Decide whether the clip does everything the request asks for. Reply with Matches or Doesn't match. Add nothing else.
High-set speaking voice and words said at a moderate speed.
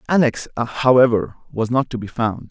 Doesn't match